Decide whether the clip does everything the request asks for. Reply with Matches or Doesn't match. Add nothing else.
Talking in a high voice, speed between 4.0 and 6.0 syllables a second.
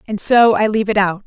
Doesn't match